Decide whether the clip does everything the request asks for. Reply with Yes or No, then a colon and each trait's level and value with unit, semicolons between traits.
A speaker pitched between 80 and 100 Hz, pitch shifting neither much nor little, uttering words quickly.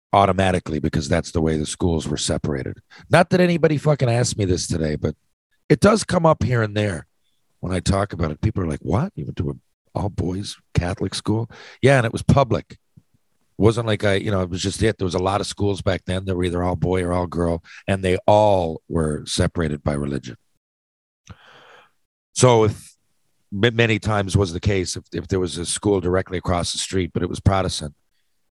Yes: very low, 95 Hz; average, 4.0 semitones; fast, 210 wpm